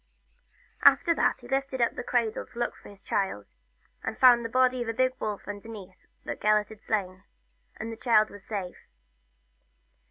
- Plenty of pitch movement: No, average, 3.1 semitones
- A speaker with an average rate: Yes, average, 180 wpm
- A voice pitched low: No, high, 225 Hz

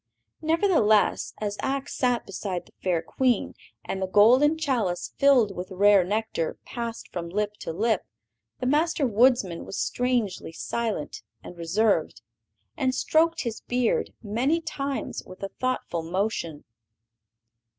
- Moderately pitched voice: No, high, 220 Hz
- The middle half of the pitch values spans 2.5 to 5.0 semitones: No, wide, 5.6 semitones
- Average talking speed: No, slow, 130 wpm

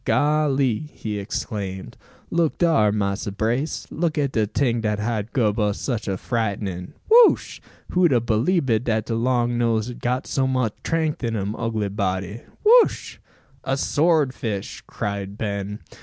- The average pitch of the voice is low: Yes, low, 115 Hz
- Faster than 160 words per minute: No, average, 155 wpm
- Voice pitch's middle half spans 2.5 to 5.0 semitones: Yes, average, 4.7 semitones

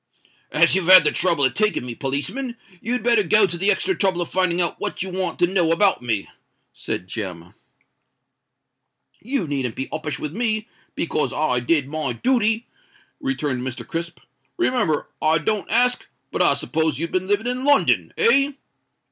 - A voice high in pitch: No, medium, 175 Hz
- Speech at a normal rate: Yes, average, 165 wpm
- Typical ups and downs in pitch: No, wide, 6.8 semitones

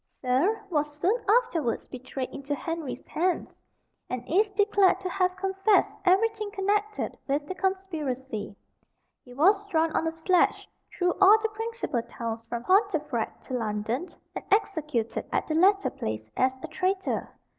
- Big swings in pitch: Yes, wide, 7.2 semitones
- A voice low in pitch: No, very high, 345 Hz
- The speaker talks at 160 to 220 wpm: No, average, 145 wpm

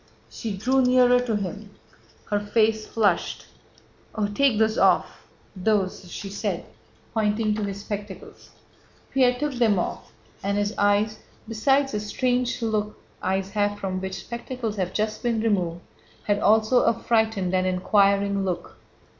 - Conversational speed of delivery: Yes, average, 145 wpm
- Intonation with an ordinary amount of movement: No, narrow, 2.3 semitones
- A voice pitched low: No, high, 210 Hz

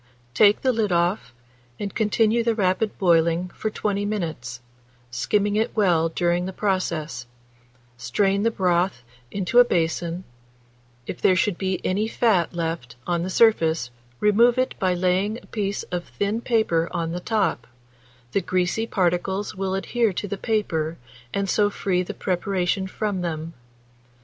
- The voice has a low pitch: No, medium, 185 Hz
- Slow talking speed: No, average, 150 wpm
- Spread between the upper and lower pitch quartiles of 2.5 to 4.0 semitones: Yes, average, 3.4 semitones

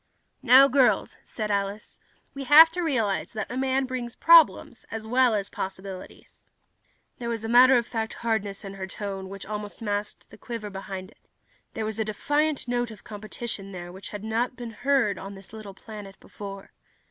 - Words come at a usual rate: Yes, average, 180 wpm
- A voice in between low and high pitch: No, high, 220 Hz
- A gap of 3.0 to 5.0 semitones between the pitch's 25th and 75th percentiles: Yes, average, 3.8 semitones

